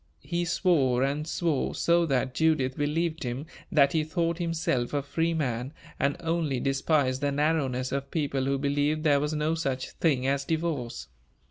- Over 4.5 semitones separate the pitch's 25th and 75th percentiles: No, average, 3.2 semitones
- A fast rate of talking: No, average, 165 wpm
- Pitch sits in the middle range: Yes, medium, 145 Hz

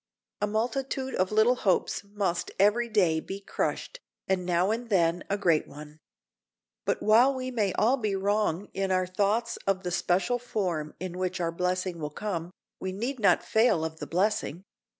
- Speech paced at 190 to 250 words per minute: No, average, 175 wpm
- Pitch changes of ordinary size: Yes, average, 3.7 semitones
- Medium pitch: No, high, 195 Hz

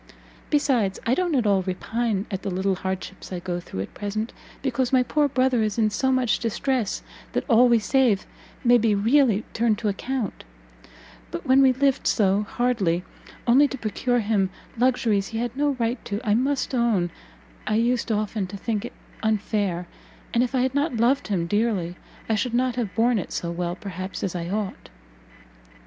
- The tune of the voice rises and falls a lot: No, average, 4.2 semitones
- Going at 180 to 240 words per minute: Yes, average, 185 wpm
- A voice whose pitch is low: No, high, 225 Hz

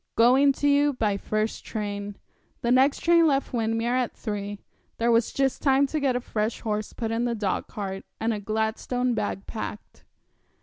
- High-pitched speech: Yes, high, 230 Hz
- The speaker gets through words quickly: No, average, 175 wpm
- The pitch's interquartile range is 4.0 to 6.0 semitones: No, average, 3.5 semitones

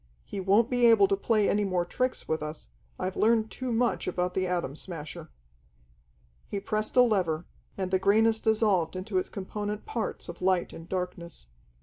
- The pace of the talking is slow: No, average, 180 wpm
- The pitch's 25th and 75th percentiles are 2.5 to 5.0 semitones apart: Yes, average, 3.4 semitones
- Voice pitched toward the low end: No, high, 195 Hz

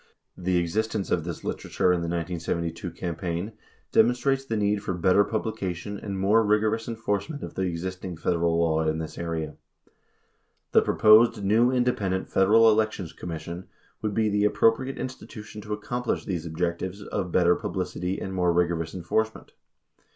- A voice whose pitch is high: No, very low, 95 Hz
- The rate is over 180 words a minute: No, average, 155 wpm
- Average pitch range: Yes, average, 4.1 semitones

